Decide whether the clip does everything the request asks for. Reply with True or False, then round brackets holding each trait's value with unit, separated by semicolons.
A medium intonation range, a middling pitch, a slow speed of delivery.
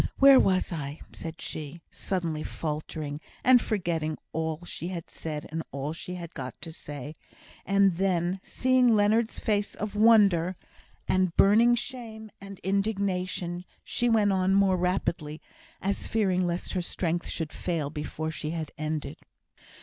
False (4.0 semitones; 180 Hz; 145 wpm)